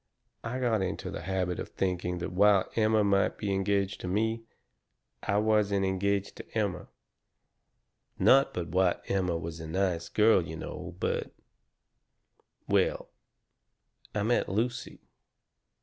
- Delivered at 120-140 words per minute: Yes, slow, 135 wpm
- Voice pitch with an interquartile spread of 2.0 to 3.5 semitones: Yes, average, 2.8 semitones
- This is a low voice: Yes, low, 100 Hz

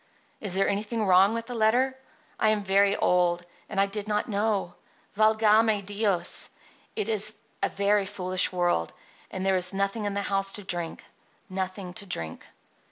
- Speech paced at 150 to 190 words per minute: Yes, average, 165 wpm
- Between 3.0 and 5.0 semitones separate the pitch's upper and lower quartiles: No, narrow, 2.4 semitones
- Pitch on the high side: Yes, high, 200 Hz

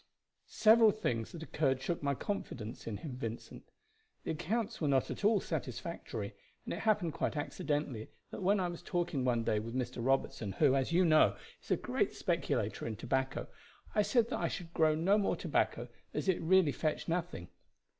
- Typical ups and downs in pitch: No, wide, 6.4 semitones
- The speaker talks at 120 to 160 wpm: No, average, 185 wpm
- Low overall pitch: No, medium, 155 Hz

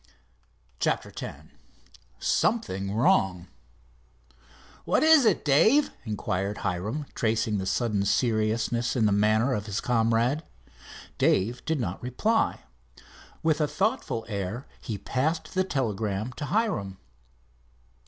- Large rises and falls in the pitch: Yes, wide, 6.3 semitones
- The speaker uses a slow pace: Yes, slow, 115 wpm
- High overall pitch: No, low, 115 Hz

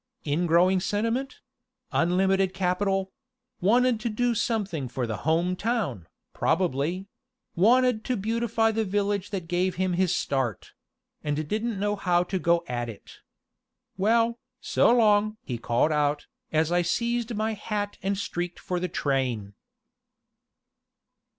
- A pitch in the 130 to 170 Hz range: No, high, 190 Hz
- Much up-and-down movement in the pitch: No, average, 4.7 semitones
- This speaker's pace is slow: Yes, slow, 130 wpm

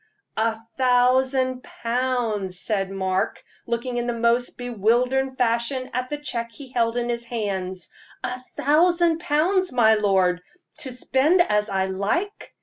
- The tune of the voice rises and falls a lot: No, average, 3.2 semitones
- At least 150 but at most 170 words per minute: No, average, 140 wpm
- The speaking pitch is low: No, high, 240 Hz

